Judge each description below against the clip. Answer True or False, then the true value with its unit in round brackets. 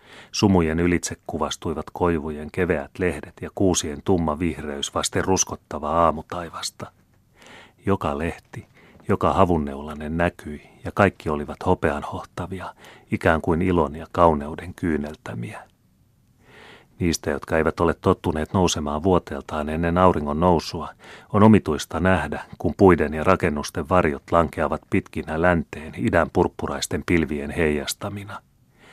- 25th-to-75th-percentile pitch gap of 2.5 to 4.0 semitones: True (3.2 semitones)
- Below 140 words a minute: True (110 wpm)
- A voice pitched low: True (85 Hz)